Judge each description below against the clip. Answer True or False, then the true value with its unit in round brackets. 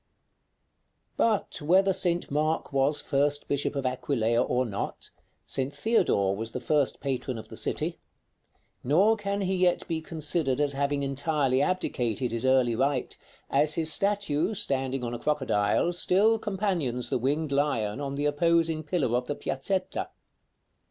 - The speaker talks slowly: False (155 wpm)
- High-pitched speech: False (145 Hz)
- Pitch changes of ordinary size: True (4.6 semitones)